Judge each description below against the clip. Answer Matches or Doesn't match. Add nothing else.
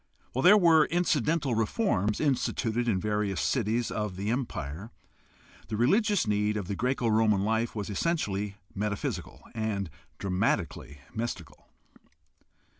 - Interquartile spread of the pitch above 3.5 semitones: Matches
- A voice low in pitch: Matches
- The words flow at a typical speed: Doesn't match